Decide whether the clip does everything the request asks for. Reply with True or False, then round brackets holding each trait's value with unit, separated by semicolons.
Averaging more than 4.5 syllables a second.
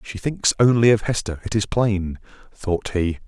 False (4.4 syllables/s)